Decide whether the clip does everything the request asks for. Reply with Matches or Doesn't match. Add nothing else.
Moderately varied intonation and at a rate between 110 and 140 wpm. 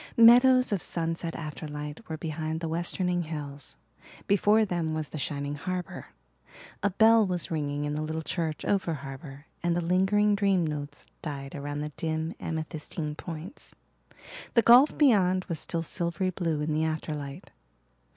Doesn't match